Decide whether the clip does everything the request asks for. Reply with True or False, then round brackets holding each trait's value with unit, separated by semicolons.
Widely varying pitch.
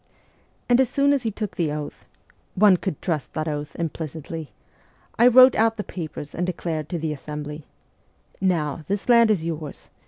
True (5.9 semitones)